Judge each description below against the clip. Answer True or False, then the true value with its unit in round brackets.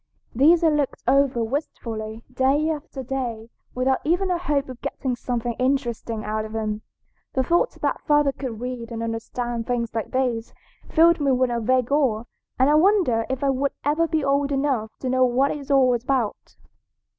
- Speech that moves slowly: False (185 wpm)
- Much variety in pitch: False (3.5 semitones)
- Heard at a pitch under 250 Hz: False (260 Hz)